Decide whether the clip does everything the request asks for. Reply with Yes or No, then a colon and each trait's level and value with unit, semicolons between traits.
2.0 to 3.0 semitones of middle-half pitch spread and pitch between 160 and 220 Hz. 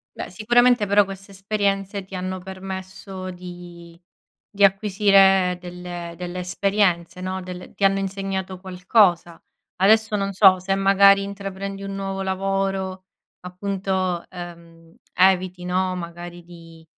No: narrow, 1.6 semitones; high, 190 Hz